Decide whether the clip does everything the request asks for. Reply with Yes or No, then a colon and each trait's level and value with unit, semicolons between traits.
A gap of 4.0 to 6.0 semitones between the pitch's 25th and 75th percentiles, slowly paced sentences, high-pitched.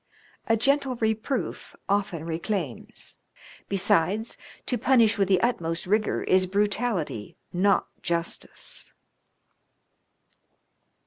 Yes: average, 4.4 semitones; slow, 85 wpm; high, 200 Hz